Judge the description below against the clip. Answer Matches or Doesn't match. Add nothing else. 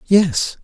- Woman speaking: Doesn't match